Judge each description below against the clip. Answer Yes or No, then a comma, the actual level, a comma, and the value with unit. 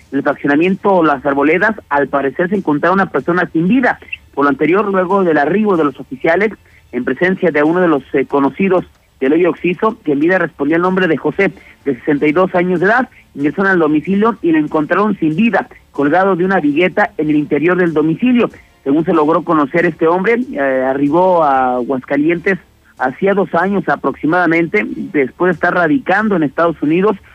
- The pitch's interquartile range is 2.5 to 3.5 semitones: No, average, 4.3 semitones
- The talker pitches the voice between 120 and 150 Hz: No, medium, 170 Hz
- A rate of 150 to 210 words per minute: Yes, average, 180 wpm